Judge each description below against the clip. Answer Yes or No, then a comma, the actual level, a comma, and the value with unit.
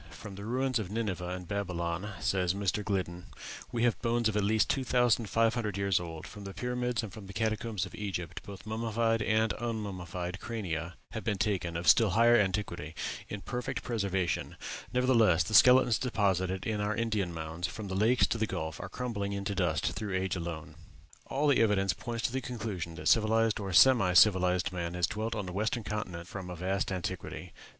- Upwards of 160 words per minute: Yes, average, 190 wpm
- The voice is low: Yes, low, 100 Hz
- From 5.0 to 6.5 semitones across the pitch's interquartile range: No, average, 3.9 semitones